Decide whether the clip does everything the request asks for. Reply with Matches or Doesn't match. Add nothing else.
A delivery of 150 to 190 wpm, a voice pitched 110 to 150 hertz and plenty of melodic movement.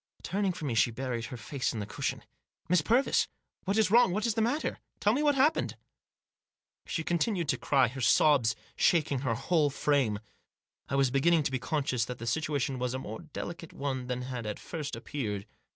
Doesn't match